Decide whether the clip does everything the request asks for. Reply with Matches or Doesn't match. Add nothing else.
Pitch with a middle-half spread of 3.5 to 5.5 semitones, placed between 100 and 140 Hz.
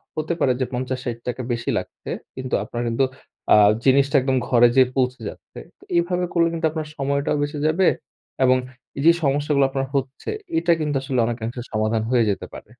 Doesn't match